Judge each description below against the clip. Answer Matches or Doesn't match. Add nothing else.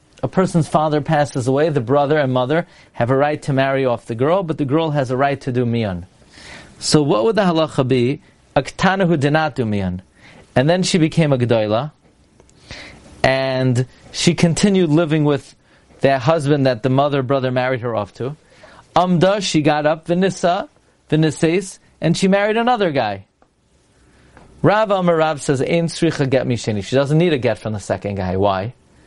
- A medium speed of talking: Matches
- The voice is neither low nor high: Matches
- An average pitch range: Matches